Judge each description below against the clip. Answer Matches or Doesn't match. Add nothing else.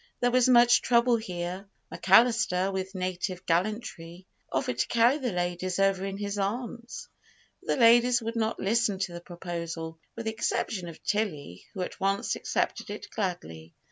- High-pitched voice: Matches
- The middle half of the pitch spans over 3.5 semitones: Matches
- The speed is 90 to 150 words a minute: Doesn't match